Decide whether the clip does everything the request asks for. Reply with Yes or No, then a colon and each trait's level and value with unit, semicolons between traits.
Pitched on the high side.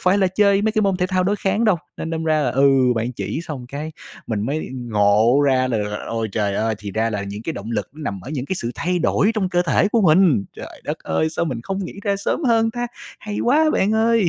No: medium, 160 Hz